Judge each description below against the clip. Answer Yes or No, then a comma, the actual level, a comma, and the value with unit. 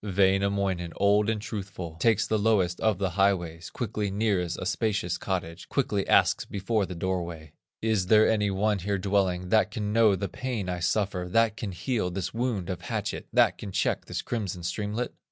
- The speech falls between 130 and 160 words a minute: No, average, 180 wpm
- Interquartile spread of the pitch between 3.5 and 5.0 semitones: No, average, 2.9 semitones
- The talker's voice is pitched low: Yes, low, 100 Hz